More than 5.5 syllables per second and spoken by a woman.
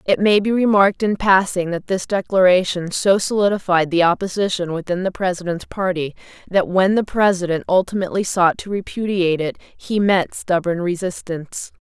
No: 5.3 syllables/s; female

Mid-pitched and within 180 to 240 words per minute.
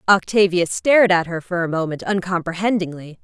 No: medium, 180 Hz; average, 150 wpm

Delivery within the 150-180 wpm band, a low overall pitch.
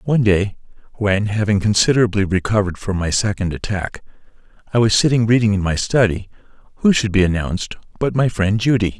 Yes: average, 165 wpm; low, 105 Hz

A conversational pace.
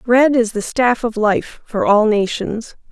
Yes: average, 185 wpm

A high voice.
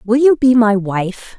Yes: high, 230 Hz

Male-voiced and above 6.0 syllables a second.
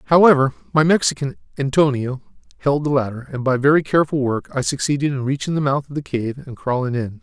Yes: male; 6.2 syllables/s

